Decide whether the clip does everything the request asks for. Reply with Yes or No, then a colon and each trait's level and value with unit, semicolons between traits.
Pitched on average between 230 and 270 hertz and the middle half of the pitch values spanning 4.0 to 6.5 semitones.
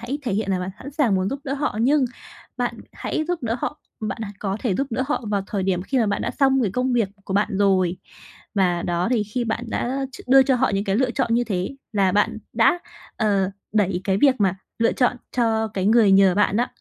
No: high, 220 Hz; average, 4.6 semitones